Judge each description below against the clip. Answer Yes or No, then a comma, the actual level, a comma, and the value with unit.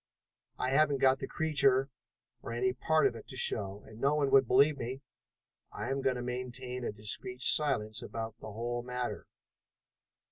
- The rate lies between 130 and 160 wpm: No, average, 175 wpm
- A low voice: Yes, low, 125 Hz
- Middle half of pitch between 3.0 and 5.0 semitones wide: No, narrow, 2.6 semitones